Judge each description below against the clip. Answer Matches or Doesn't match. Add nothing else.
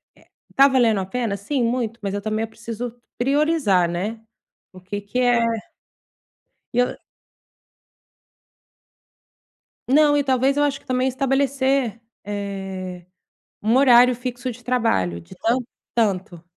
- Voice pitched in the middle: Doesn't match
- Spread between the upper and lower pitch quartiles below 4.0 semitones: Doesn't match